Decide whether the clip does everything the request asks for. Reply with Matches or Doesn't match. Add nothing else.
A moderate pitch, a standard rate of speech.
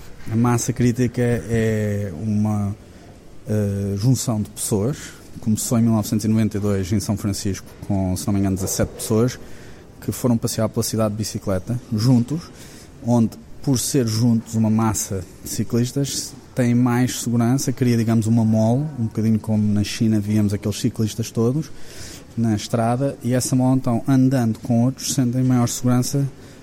Doesn't match